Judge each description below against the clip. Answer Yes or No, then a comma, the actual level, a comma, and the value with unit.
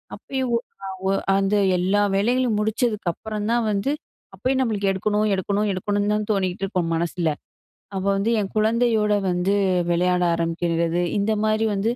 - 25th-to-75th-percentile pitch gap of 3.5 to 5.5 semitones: No, average, 2.9 semitones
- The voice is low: No, high, 205 Hz